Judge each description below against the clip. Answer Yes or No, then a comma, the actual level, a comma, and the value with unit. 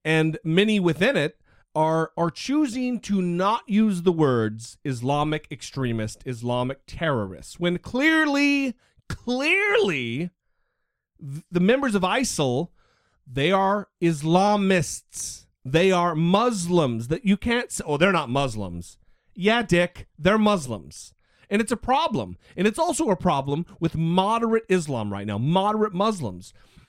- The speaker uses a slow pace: Yes, slow, 125 wpm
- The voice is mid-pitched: Yes, medium, 175 Hz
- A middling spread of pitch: No, wide, 7.5 semitones